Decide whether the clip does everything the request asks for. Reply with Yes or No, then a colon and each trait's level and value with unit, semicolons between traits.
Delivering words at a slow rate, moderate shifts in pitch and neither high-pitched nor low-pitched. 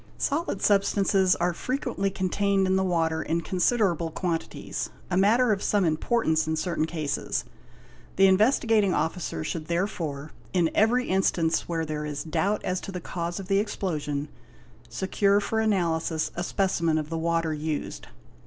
No: average, 155 wpm; average, 3.6 semitones; medium, 180 Hz